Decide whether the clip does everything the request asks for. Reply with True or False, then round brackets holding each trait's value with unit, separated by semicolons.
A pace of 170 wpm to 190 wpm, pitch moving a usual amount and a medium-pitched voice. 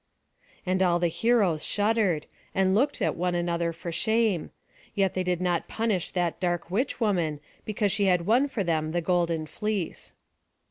True (175 wpm; 3.6 semitones; 180 Hz)